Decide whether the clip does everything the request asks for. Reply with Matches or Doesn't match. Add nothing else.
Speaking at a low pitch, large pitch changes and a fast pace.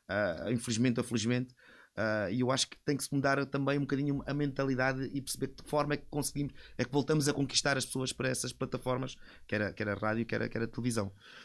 Doesn't match